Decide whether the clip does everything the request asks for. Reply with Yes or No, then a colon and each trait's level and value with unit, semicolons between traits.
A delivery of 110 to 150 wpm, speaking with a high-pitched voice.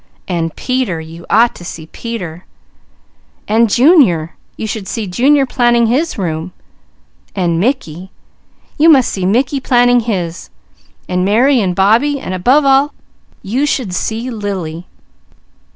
Yes: slow, 135 wpm; high, 220 Hz